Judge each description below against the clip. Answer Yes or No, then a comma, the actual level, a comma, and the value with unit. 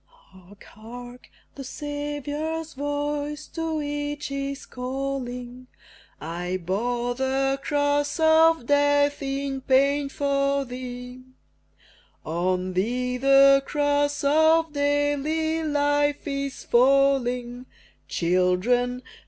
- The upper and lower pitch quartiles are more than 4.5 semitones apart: No, average, 2.8 semitones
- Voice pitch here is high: Yes, very high, 275 Hz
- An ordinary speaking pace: No, slow, 90 wpm